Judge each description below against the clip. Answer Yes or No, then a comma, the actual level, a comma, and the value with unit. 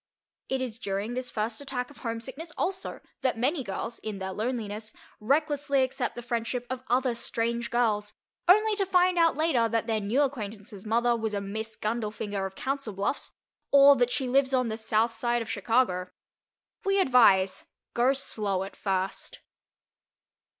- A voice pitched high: Yes, high, 235 Hz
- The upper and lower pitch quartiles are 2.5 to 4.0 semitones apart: Yes, average, 3.7 semitones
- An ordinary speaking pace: Yes, average, 165 wpm